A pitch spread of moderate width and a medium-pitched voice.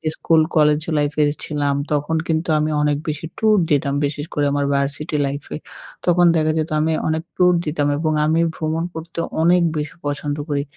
No: narrow, 1.8 semitones; medium, 150 Hz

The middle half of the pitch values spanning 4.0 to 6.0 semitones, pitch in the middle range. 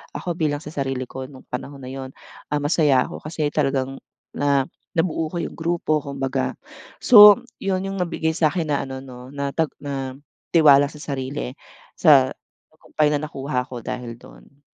No: average, 3.1 semitones; medium, 145 Hz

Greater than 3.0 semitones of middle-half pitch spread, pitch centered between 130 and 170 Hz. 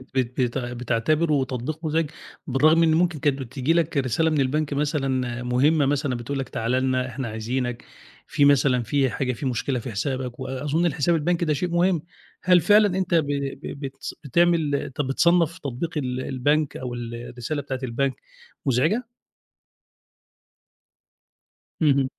Yes: average, 3.7 semitones; medium, 140 Hz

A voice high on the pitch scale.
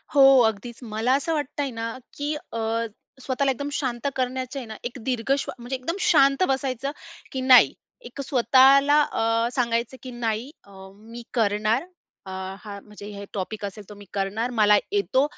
Yes: high, 240 Hz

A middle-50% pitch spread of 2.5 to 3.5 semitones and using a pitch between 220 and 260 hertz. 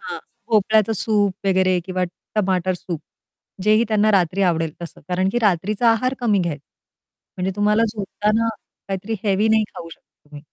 No: average, 2.9 semitones; high, 195 Hz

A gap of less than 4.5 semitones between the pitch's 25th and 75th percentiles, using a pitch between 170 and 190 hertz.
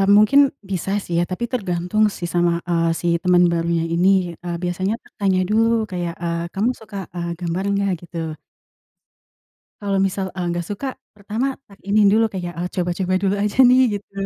Yes: average, 2.8 semitones; medium, 185 Hz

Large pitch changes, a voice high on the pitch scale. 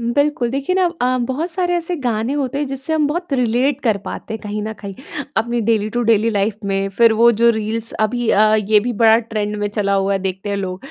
No: average, 4.0 semitones; high, 230 Hz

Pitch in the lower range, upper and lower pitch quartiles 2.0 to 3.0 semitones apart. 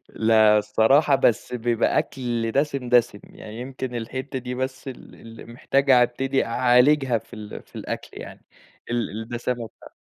Yes: low, 120 Hz; narrow, 2.5 semitones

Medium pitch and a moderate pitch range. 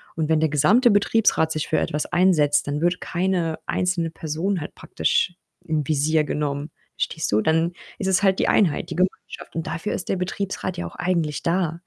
Yes: medium, 165 Hz; average, 3.1 semitones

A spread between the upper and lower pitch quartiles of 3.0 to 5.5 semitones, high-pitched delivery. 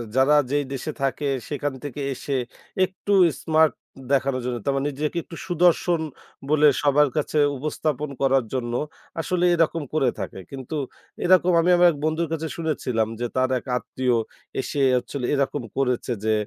No: average, 3.3 semitones; medium, 145 Hz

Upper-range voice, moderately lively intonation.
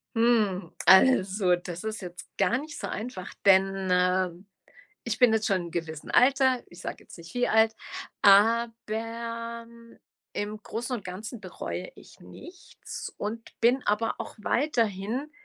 Yes: high, 220 Hz; average, 3.7 semitones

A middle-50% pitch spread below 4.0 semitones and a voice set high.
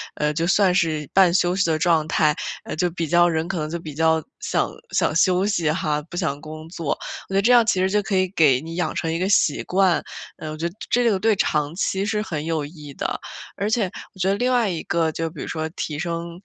No: average, 3.4 semitones; medium, 170 Hz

